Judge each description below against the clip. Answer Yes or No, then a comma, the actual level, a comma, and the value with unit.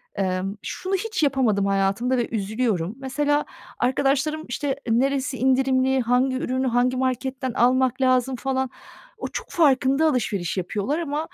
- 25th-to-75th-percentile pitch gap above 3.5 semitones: No, narrow, 2.5 semitones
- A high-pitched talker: Yes, very high, 260 Hz